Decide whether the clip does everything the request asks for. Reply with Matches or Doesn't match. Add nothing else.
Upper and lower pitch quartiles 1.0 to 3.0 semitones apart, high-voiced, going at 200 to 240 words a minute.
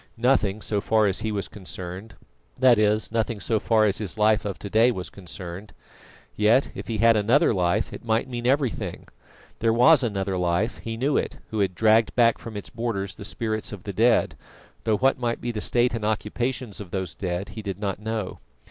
Doesn't match